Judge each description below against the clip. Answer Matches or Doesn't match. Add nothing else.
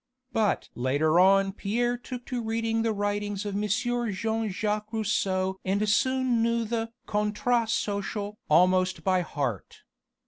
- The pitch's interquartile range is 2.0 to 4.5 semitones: Matches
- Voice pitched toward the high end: Matches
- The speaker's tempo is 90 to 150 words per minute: Matches